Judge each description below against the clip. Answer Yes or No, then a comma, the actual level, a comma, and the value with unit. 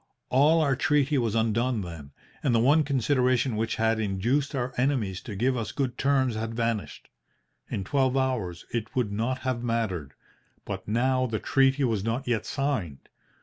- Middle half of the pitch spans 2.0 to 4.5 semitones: Yes, average, 3.3 semitones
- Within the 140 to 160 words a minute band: No, average, 170 wpm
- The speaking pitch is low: Yes, low, 120 Hz